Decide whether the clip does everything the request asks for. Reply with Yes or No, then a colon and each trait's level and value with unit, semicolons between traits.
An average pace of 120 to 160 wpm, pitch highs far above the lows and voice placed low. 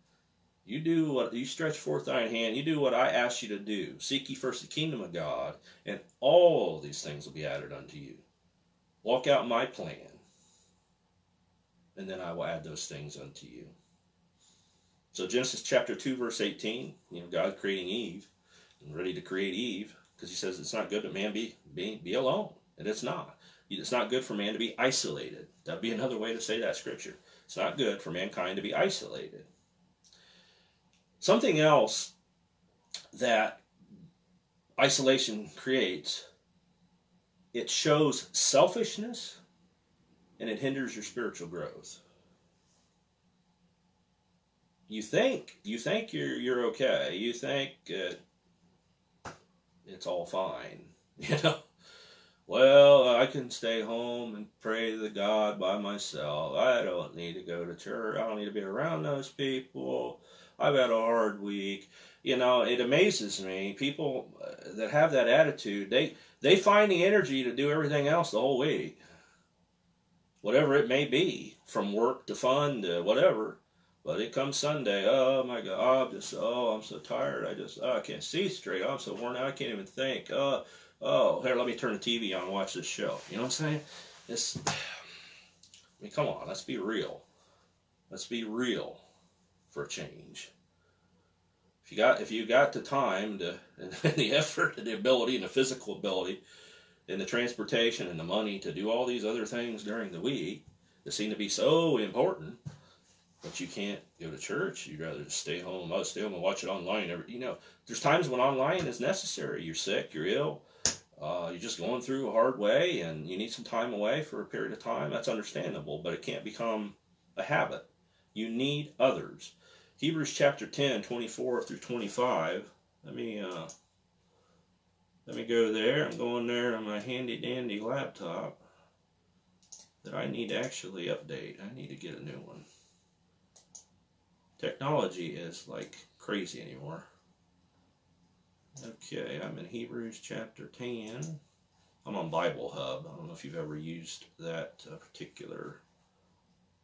No: average, 170 wpm; wide, 5.7 semitones; low, 115 Hz